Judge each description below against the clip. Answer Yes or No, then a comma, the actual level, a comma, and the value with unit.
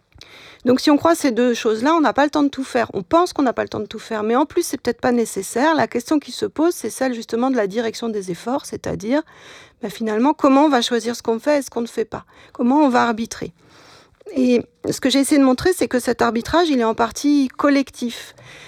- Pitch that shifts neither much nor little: Yes, average, 4.1 semitones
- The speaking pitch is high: Yes, very high, 250 Hz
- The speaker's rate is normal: No, fast, 260 wpm